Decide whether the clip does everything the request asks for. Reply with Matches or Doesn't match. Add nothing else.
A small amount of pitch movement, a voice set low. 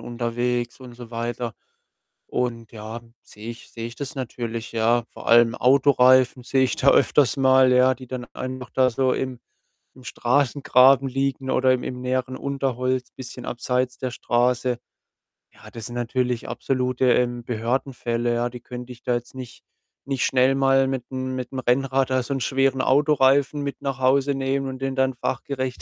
Matches